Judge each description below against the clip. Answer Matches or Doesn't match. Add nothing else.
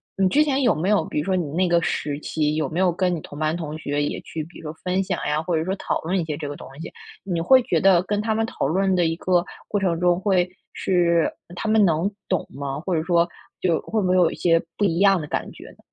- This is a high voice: Doesn't match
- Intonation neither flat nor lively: Matches